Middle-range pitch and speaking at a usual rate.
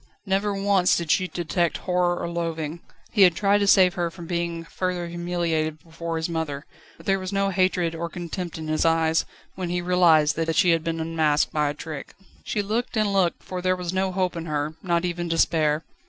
No: medium, 170 Hz; fast, 210 wpm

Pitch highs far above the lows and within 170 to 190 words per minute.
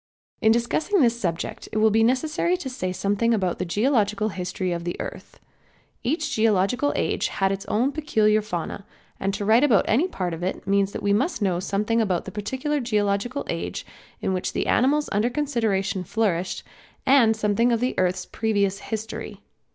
No: average, 4.1 semitones; average, 180 wpm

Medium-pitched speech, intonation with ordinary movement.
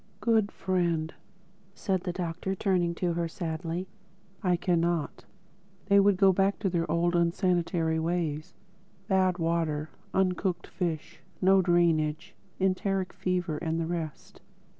No: medium, 175 Hz; narrow, 2.2 semitones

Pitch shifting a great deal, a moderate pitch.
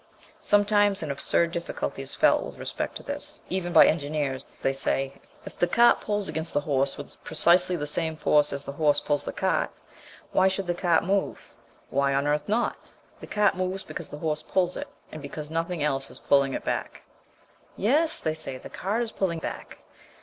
No: average, 4.6 semitones; medium, 160 Hz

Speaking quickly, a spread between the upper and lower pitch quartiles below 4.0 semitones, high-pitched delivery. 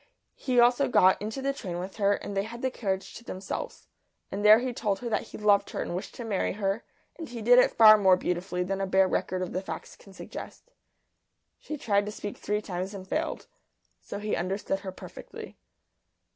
Yes: fast, 215 wpm; average, 3.6 semitones; high, 205 Hz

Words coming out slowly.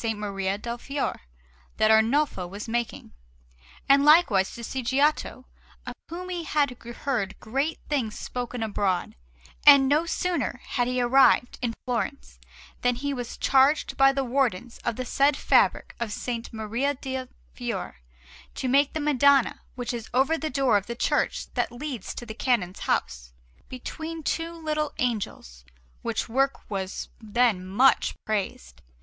No: average, 150 wpm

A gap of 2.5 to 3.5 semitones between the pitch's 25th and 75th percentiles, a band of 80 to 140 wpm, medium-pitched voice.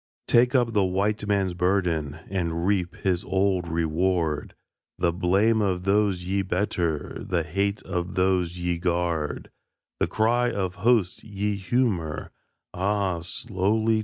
No: average, 2.8 semitones; slow, 135 wpm; very low, 95 Hz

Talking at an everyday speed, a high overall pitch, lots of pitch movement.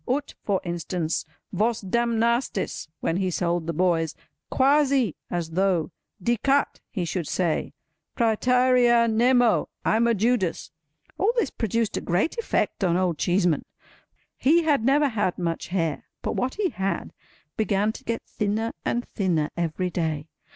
No: slow, 130 wpm; high, 205 Hz; wide, 5.7 semitones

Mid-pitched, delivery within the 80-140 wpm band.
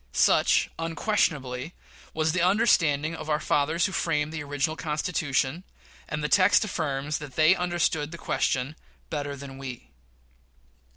Yes: medium, 155 Hz; slow, 135 wpm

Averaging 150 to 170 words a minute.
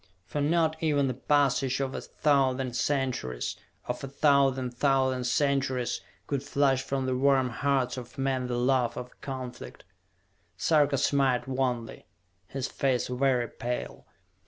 No: slow, 135 wpm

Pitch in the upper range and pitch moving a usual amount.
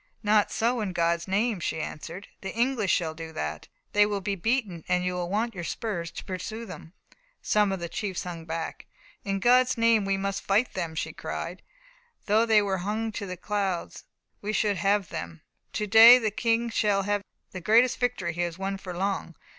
Yes: high, 195 Hz; average, 3.7 semitones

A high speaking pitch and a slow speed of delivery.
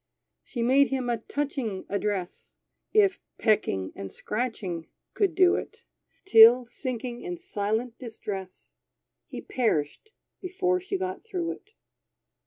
Yes: very high, 250 Hz; slow, 120 wpm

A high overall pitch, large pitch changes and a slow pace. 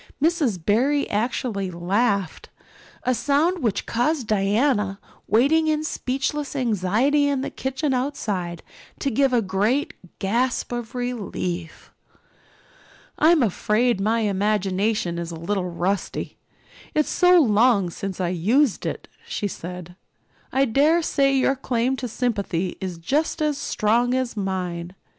Yes: high, 230 Hz; wide, 6.0 semitones; slow, 130 wpm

